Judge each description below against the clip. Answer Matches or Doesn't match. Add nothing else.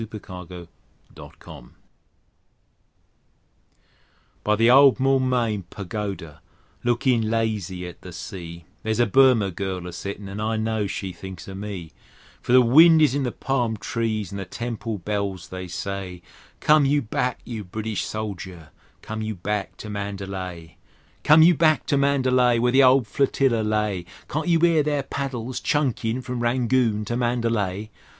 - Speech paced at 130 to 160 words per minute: Matches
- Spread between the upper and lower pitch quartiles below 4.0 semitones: Doesn't match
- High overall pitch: Doesn't match